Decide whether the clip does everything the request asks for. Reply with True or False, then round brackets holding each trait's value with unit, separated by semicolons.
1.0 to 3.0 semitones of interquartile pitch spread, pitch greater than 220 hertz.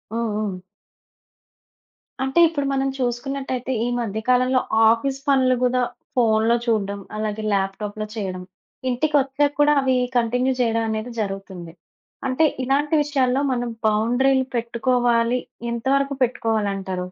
False (3.4 semitones; 245 Hz)